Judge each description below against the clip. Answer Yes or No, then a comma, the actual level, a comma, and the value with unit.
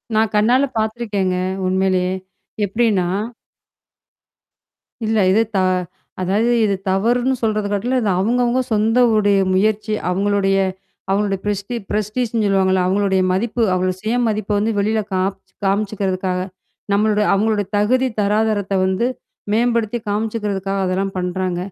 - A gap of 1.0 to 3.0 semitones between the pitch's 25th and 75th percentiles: Yes, narrow, 2.4 semitones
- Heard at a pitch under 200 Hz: No, high, 205 Hz